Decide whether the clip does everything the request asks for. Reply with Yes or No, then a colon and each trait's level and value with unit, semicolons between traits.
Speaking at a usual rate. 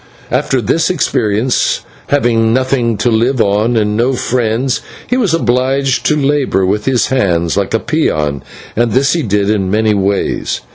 Yes: average, 160 wpm